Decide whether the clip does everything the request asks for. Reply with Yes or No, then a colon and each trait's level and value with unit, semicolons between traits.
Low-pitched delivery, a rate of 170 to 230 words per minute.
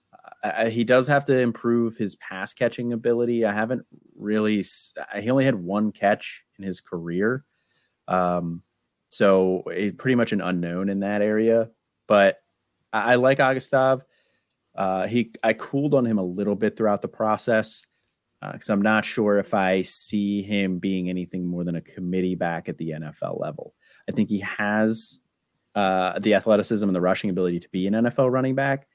Yes: low, 105 Hz; average, 175 wpm